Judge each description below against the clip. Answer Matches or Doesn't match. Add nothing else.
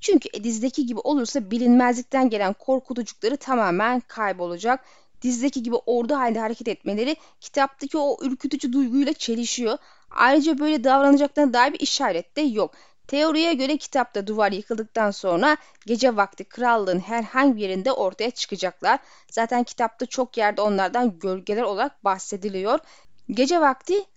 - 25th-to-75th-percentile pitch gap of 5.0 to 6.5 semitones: Doesn't match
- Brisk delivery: Doesn't match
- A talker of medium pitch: Doesn't match